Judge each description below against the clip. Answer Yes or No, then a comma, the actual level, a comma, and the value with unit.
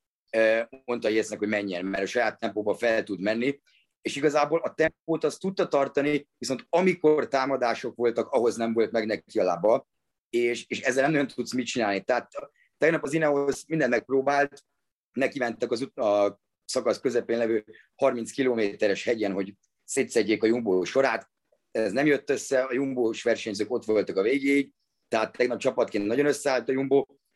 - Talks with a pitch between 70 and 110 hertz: No, low, 125 Hz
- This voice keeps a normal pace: No, fast, 170 wpm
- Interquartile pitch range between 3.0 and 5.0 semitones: Yes, average, 4.1 semitones